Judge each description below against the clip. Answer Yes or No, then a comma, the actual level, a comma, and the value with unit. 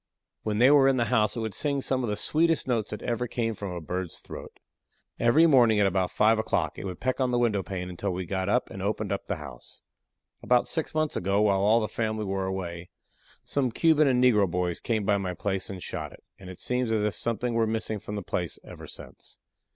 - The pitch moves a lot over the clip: No, average, 4.2 semitones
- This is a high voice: No, low, 110 Hz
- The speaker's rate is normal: No, fast, 235 wpm